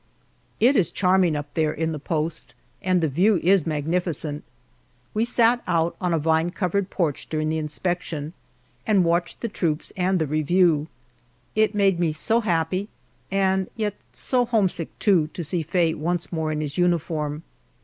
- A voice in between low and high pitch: Yes, medium, 170 Hz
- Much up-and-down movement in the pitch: No, average, 3.4 semitones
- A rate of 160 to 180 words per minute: Yes, average, 165 wpm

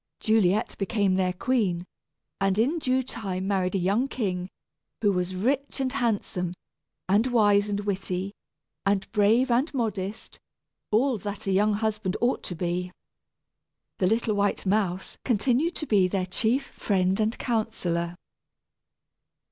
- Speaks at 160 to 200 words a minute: No, average, 140 wpm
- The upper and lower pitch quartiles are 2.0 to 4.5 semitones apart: Yes, average, 3.6 semitones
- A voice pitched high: Yes, high, 205 Hz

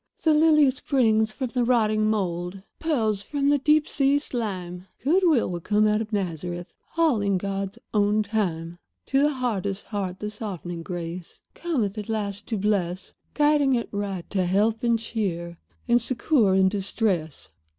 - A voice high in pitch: Yes, high, 210 Hz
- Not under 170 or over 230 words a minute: No, average, 160 wpm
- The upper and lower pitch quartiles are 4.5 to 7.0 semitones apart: Yes, average, 4.8 semitones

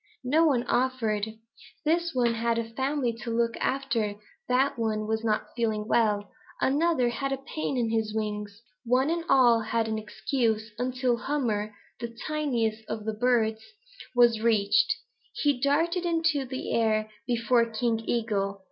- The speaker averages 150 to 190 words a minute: Yes, average, 155 wpm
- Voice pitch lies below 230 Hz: No, high, 235 Hz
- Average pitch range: Yes, average, 3.3 semitones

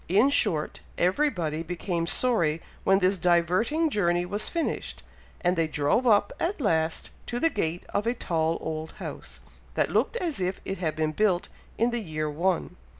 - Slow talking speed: No, average, 170 wpm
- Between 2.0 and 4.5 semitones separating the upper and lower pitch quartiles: No, wide, 5.6 semitones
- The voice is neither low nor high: Yes, medium, 180 Hz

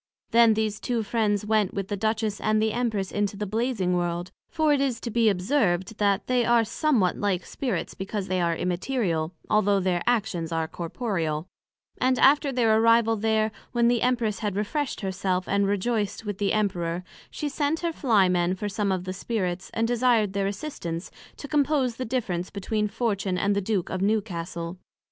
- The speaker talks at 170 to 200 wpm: Yes, average, 185 wpm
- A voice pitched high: Yes, high, 210 Hz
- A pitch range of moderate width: Yes, average, 4.0 semitones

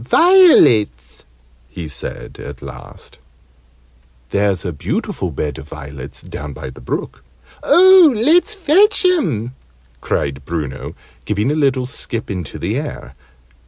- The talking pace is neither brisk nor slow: No, slow, 125 wpm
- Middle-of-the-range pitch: No, low, 105 Hz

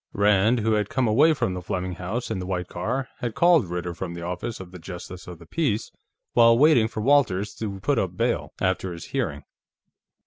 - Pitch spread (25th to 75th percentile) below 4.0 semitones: No, average, 4.8 semitones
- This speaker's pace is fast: Yes, fast, 210 wpm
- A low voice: Yes, low, 100 Hz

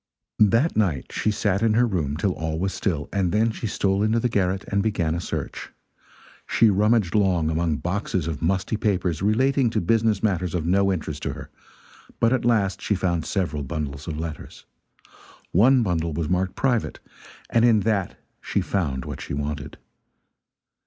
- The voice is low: Yes, very low, 95 Hz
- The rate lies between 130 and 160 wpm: No, average, 175 wpm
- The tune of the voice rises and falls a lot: No, average, 4.8 semitones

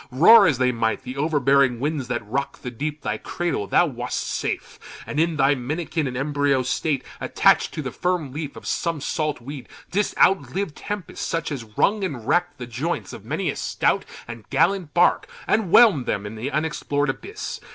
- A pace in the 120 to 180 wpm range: No, average, 190 wpm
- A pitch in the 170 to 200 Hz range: No, medium, 145 Hz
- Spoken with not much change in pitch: No, average, 4.9 semitones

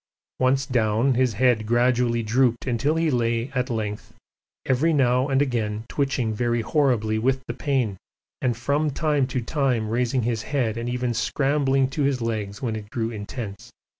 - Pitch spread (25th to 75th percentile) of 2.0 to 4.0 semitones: Yes, average, 3.1 semitones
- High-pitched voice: No, low, 125 Hz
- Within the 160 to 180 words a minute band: Yes, average, 165 wpm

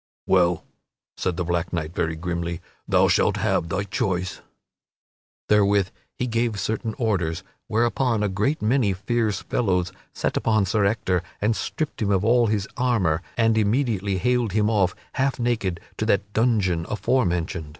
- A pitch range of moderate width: Yes, average, 4.0 semitones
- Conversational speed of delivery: Yes, average, 150 wpm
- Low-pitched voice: Yes, low, 100 Hz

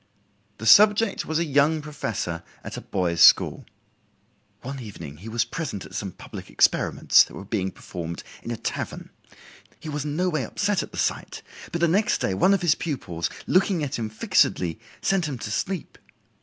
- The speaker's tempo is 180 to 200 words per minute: Yes, average, 185 wpm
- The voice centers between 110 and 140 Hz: Yes, low, 135 Hz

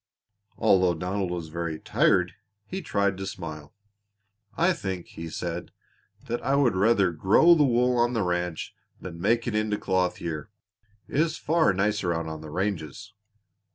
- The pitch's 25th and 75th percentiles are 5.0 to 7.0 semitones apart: Yes, average, 5.3 semitones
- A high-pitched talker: No, very low, 95 Hz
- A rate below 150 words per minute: No, average, 160 wpm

